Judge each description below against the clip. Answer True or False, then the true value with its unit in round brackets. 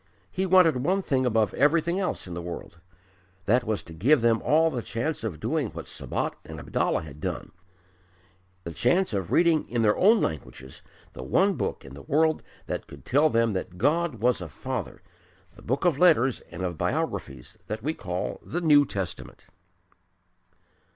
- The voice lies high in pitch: False (120 Hz)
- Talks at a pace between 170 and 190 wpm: True (180 wpm)